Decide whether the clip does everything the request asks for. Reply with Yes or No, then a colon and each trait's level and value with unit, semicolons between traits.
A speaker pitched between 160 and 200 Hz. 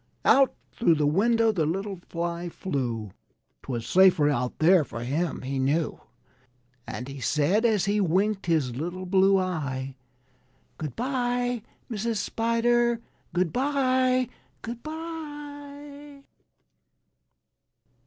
Yes: high, 190 Hz